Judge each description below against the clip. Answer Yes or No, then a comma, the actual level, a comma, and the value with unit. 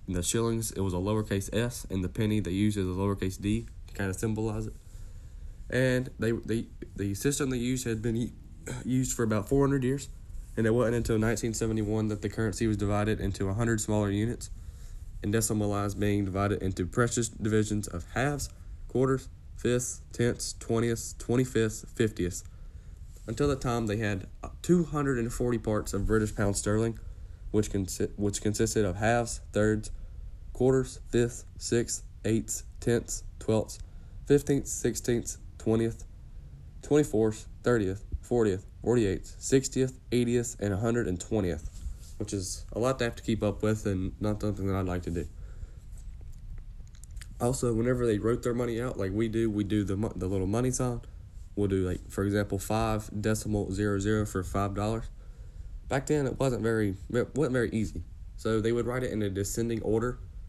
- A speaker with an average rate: Yes, average, 170 wpm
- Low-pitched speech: Yes, low, 105 Hz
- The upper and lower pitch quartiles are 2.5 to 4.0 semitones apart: Yes, average, 3.4 semitones